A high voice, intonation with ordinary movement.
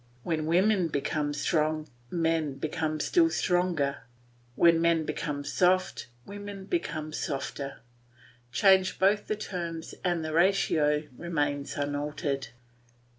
No: medium, 160 Hz; average, 3.7 semitones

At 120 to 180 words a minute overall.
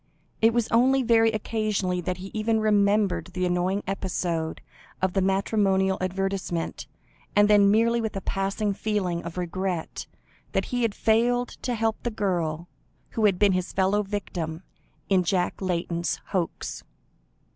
Yes: average, 145 wpm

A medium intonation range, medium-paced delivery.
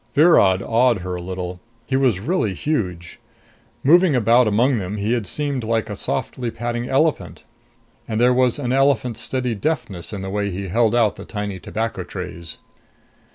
Yes: average, 4.8 semitones; average, 170 wpm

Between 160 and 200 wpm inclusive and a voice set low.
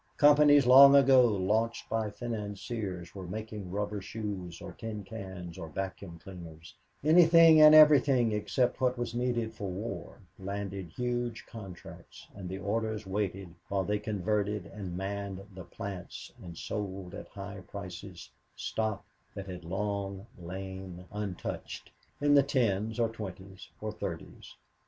No: slow, 135 wpm; low, 100 Hz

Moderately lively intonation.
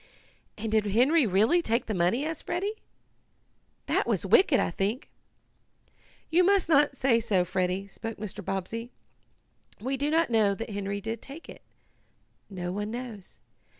No: wide, 5.8 semitones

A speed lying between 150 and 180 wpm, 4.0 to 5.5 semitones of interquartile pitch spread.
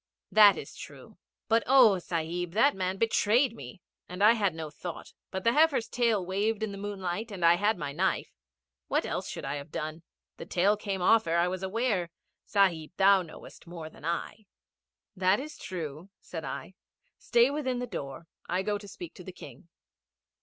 No: average, 190 wpm; average, 4.3 semitones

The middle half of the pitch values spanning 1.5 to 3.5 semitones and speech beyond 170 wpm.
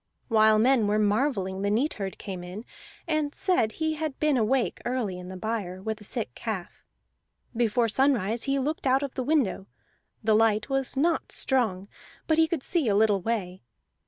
No: average, 4.9 semitones; average, 180 wpm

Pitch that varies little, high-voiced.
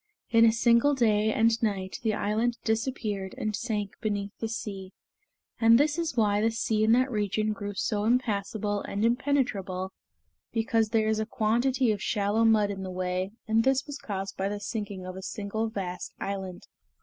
Yes: narrow, 2.3 semitones; high, 215 Hz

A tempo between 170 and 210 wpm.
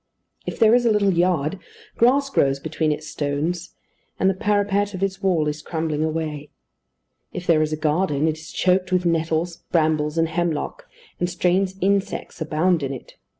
Yes: average, 175 wpm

